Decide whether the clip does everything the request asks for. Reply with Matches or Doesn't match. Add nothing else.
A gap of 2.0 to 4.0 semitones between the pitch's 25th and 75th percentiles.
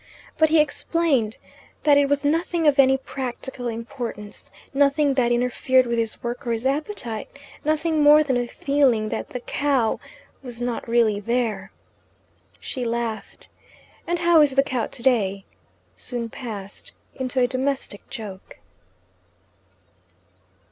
Matches